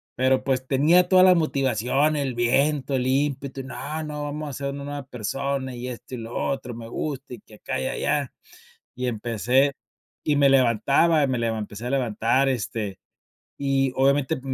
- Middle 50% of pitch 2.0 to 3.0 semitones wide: Yes, average, 2.7 semitones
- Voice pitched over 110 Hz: Yes, low, 135 Hz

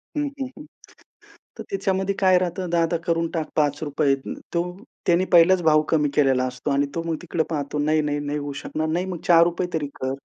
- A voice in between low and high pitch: Yes, medium, 165 Hz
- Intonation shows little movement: No, average, 3.2 semitones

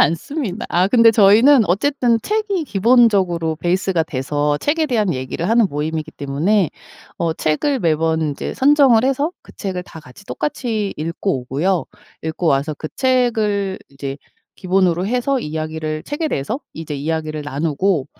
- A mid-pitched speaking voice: Yes, medium, 180 Hz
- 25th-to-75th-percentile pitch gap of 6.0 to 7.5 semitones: Yes, wide, 7.1 semitones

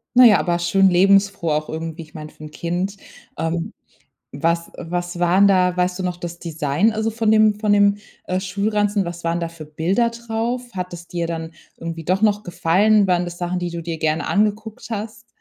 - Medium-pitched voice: Yes, medium, 180 Hz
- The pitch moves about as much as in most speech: Yes, average, 3.6 semitones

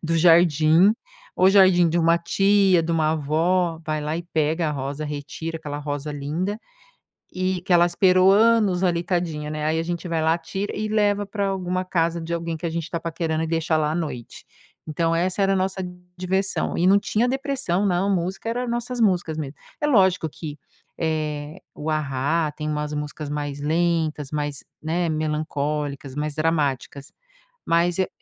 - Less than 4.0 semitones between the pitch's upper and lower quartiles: Yes, average, 3.3 semitones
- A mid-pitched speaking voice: Yes, medium, 165 Hz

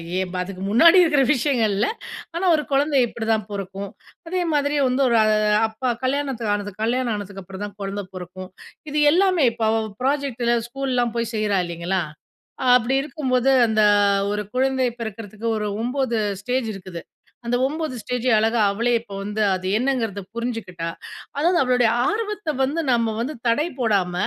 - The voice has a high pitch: Yes, high, 235 Hz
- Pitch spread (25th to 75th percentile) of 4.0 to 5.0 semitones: Yes, average, 4.7 semitones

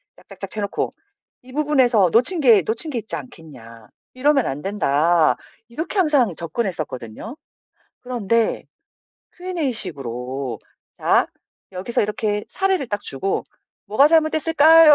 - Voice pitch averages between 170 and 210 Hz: No, high, 225 Hz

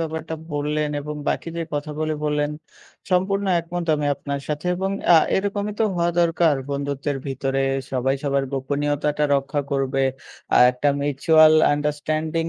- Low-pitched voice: No, medium, 150 Hz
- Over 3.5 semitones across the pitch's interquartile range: No, narrow, 2.6 semitones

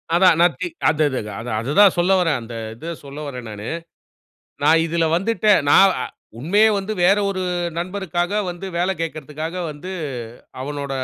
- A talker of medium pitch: Yes, medium, 170 Hz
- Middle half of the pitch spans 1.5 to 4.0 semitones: No, average, 4.6 semitones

